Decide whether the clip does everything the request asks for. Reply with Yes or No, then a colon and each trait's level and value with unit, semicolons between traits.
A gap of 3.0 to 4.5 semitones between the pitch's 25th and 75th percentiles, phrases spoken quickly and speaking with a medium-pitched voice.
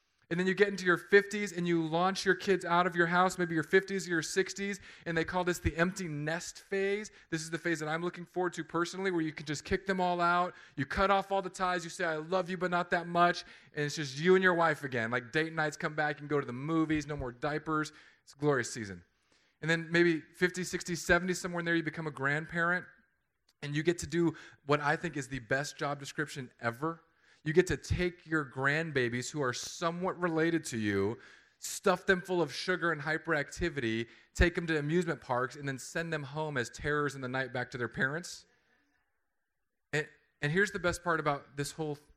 Yes: average, 3.4 semitones; fast, 230 wpm; medium, 165 Hz